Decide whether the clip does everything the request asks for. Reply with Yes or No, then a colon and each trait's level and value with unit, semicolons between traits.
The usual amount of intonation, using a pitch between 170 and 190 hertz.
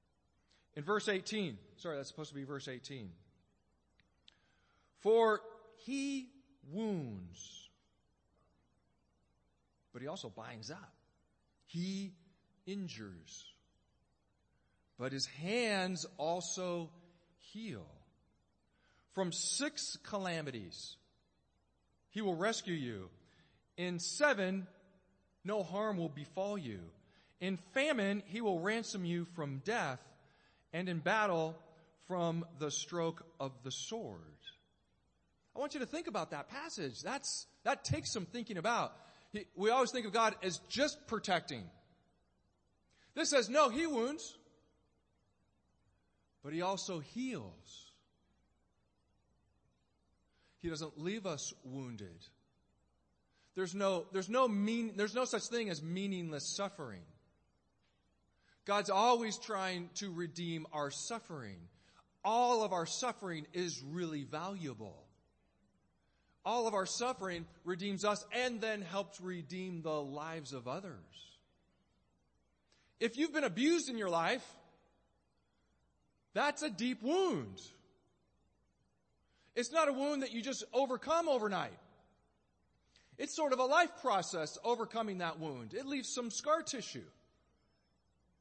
No: wide, 6.8 semitones; medium, 185 Hz